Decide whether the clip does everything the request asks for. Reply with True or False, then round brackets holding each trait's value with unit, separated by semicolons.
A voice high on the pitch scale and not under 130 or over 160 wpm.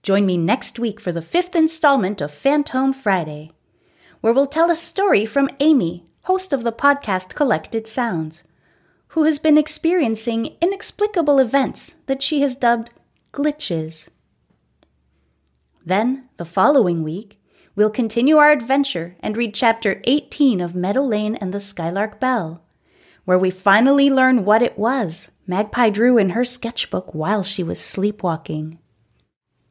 True (230 Hz; 140 wpm)